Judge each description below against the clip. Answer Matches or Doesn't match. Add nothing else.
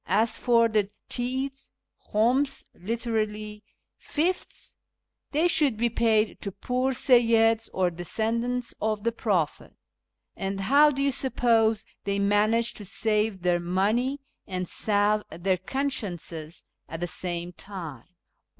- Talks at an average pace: Doesn't match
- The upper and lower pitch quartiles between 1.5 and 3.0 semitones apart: Doesn't match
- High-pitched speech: Matches